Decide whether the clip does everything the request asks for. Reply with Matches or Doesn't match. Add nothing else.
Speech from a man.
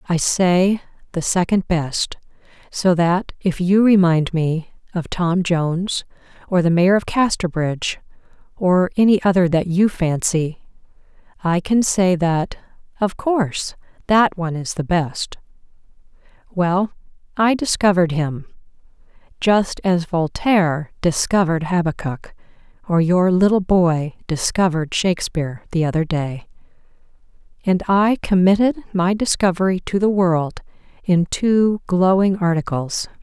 Doesn't match